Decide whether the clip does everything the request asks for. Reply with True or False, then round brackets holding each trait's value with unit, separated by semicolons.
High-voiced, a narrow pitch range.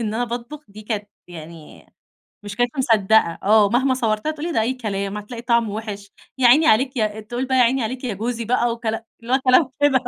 False (230 Hz; 3.2 semitones)